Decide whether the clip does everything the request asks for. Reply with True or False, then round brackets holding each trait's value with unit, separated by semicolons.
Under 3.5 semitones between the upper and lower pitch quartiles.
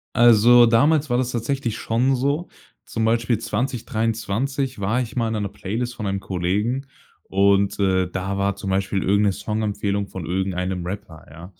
False (3.8 semitones)